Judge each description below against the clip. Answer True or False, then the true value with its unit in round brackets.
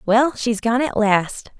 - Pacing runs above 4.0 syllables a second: False (3.6 syllables/s)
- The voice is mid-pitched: False (230 Hz)